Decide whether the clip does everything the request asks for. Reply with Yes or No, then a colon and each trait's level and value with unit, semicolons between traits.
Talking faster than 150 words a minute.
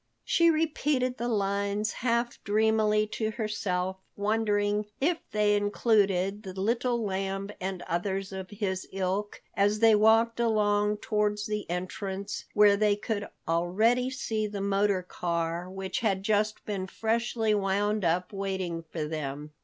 No: slow, 135 wpm